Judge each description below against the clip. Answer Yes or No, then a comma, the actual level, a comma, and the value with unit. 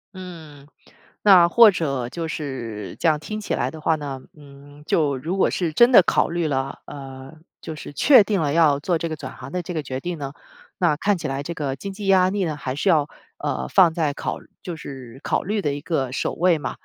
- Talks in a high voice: No, medium, 155 Hz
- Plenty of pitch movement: No, average, 4.3 semitones